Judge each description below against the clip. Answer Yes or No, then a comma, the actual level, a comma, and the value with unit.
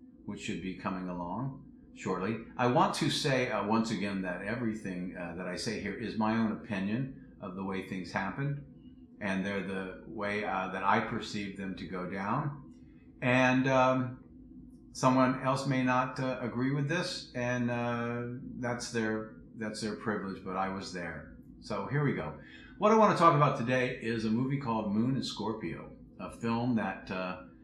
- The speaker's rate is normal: Yes, average, 180 wpm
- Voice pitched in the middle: No, low, 115 Hz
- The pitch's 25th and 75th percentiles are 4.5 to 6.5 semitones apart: Yes, average, 4.8 semitones